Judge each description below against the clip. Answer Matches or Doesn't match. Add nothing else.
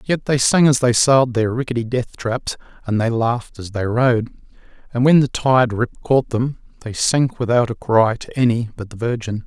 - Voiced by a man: Matches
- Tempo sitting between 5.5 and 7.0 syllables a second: Doesn't match